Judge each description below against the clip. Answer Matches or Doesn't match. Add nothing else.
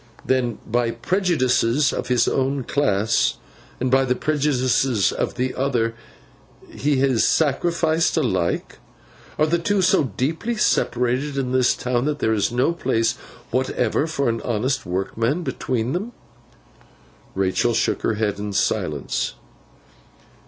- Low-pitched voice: Matches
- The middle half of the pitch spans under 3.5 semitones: Doesn't match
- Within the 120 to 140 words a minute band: Matches